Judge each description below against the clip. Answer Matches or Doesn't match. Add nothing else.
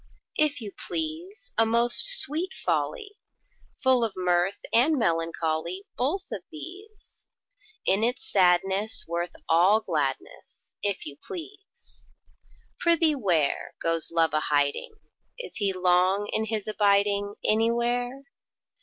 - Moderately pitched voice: Doesn't match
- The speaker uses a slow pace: Matches